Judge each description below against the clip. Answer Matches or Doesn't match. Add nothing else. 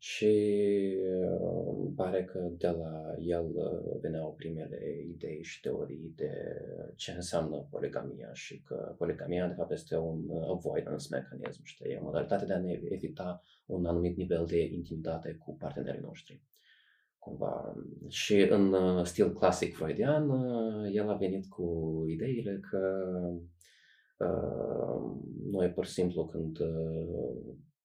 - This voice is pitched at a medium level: Doesn't match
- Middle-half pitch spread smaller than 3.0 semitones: Matches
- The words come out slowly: Doesn't match